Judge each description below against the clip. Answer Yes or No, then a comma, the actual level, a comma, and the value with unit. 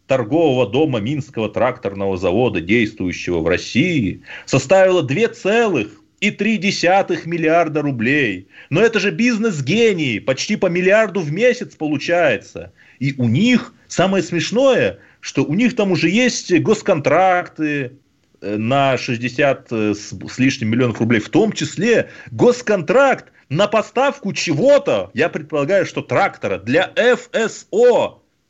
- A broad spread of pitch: Yes, wide, 8.0 semitones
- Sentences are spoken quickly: No, average, 115 wpm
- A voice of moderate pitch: Yes, medium, 170 Hz